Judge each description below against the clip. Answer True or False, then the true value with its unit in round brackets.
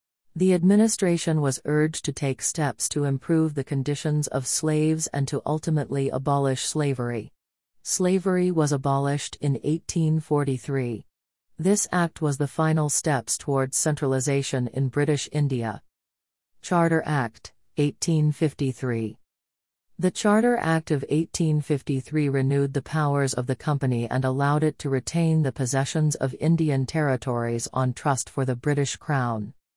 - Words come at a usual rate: False (130 wpm)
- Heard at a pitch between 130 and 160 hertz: True (140 Hz)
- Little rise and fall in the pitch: False (3.1 semitones)